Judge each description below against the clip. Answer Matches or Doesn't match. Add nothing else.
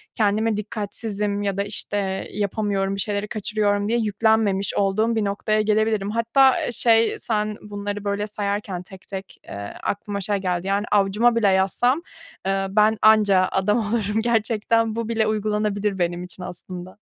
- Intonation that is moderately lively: Doesn't match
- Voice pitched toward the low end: Doesn't match